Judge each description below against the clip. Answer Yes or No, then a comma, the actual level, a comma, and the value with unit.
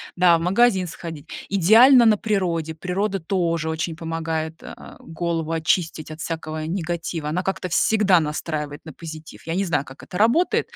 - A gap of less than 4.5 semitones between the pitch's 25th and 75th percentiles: Yes, average, 3.0 semitones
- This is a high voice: No, medium, 165 Hz